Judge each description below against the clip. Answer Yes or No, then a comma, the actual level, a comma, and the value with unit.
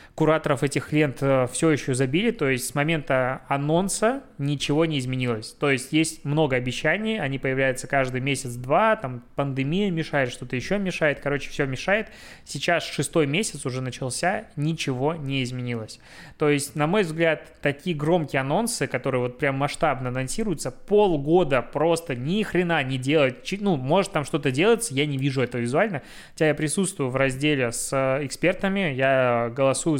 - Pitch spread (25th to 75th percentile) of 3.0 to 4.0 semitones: Yes, average, 3.7 semitones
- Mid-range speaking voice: Yes, medium, 145 Hz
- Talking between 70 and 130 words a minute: No, average, 155 wpm